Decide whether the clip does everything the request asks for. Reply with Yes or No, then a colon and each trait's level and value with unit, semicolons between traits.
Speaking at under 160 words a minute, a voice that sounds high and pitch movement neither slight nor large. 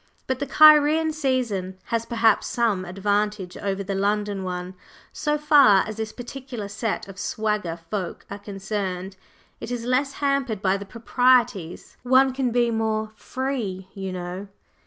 Yes: average, 150 wpm; high, 215 Hz; average, 4.7 semitones